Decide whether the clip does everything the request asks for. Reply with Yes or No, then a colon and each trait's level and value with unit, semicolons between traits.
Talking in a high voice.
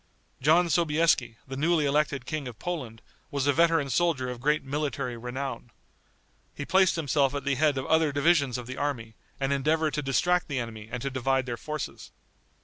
No: medium, 140 Hz